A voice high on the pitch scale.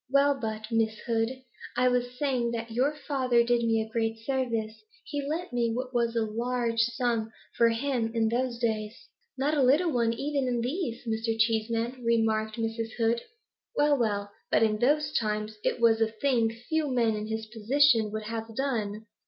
Yes: high, 235 Hz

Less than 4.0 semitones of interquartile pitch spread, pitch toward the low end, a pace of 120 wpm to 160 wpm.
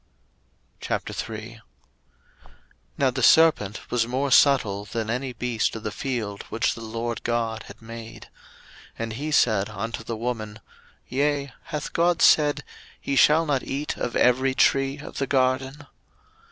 Yes: average, 3.5 semitones; low, 125 Hz; average, 140 wpm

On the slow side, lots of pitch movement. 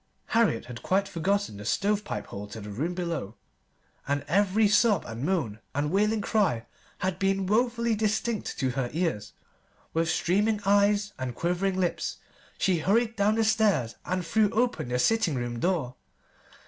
No: average, 160 wpm; wide, 6.7 semitones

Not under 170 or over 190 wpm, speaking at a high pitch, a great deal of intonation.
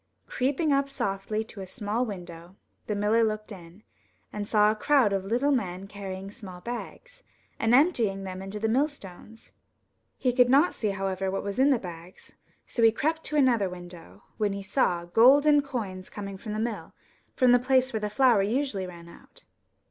No: average, 185 wpm; high, 215 Hz; average, 4.8 semitones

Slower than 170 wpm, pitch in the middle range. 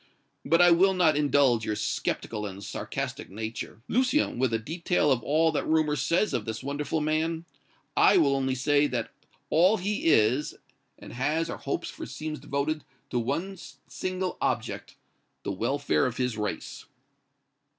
Yes: average, 160 wpm; medium, 145 Hz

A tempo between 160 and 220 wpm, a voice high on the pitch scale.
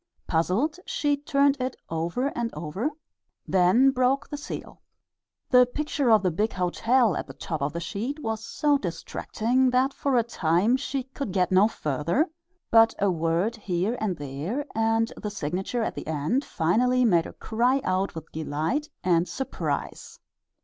Yes: average, 165 wpm; high, 220 Hz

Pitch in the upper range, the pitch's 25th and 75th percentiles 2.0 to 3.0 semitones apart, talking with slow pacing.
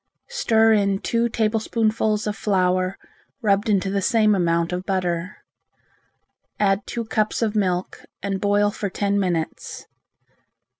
Yes: high, 200 Hz; narrow, 2.5 semitones; slow, 130 wpm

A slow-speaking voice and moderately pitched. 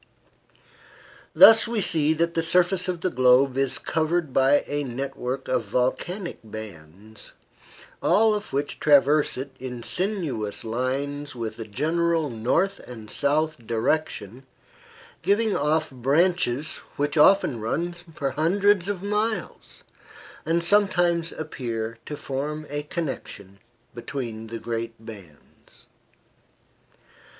Yes: slow, 115 wpm; medium, 145 Hz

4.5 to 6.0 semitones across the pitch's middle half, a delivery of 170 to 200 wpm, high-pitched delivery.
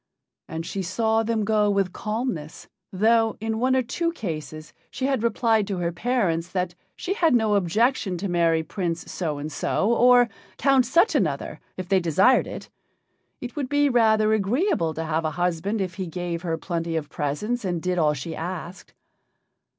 Yes: wide, 5.6 semitones; average, 180 wpm; high, 195 Hz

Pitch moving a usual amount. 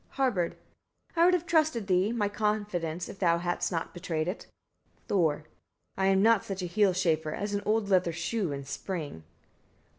Yes: average, 3.8 semitones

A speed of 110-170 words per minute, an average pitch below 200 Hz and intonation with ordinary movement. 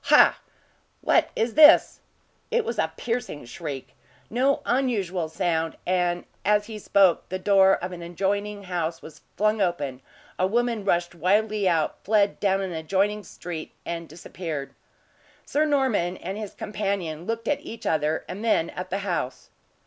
Yes: average, 155 wpm; high, 190 Hz; average, 3.8 semitones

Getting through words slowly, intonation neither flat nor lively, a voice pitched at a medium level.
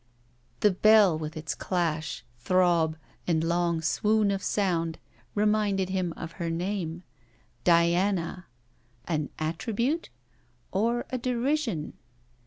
Yes: slow, 105 wpm; average, 4.1 semitones; medium, 180 Hz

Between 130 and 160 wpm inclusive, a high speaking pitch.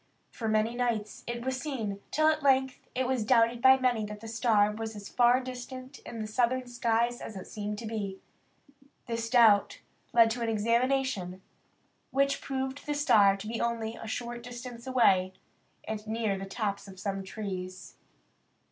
No: average, 175 wpm; high, 230 Hz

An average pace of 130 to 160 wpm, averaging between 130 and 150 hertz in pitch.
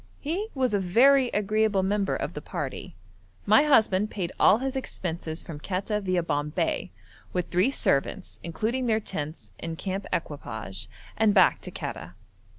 No: average, 155 wpm; high, 195 Hz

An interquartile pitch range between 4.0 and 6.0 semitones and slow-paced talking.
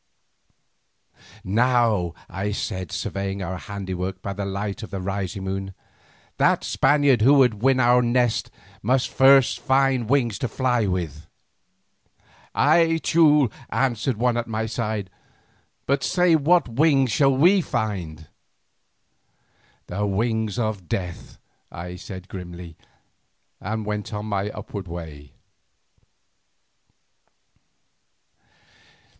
Yes: average, 5.1 semitones; slow, 110 wpm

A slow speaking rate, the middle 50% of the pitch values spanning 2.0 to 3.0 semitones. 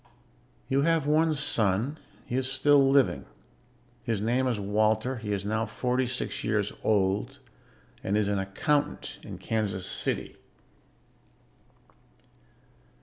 No: slow, 120 wpm; average, 4.7 semitones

